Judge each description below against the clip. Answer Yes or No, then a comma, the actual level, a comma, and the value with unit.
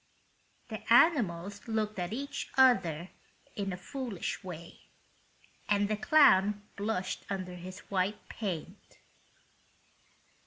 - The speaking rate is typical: No, slow, 105 wpm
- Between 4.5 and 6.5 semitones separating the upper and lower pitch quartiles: No, average, 3.3 semitones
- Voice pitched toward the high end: Yes, high, 200 Hz